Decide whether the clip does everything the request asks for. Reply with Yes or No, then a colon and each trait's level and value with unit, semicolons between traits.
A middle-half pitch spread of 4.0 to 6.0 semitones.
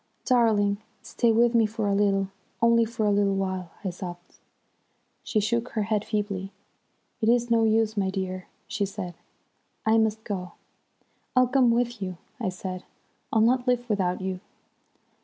No: average, 3.3 semitones